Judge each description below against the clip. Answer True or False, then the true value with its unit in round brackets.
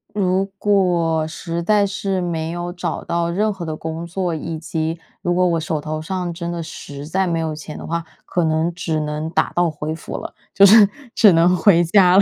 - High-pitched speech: False (170 Hz)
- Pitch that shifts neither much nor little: False (2.3 semitones)